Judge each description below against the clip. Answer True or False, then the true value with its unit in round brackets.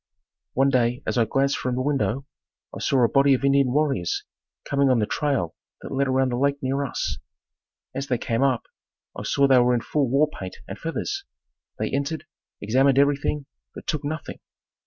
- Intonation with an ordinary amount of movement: False (2.1 semitones)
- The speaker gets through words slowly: False (190 wpm)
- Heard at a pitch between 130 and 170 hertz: True (135 Hz)